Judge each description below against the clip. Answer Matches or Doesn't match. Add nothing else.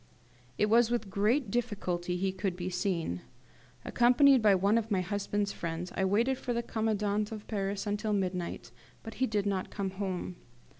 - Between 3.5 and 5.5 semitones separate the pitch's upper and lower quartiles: Doesn't match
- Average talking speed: Matches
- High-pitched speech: Matches